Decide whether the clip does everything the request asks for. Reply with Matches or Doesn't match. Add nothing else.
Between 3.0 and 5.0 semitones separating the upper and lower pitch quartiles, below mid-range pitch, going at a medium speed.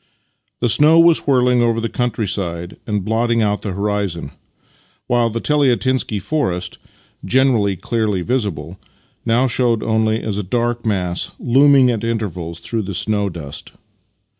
Matches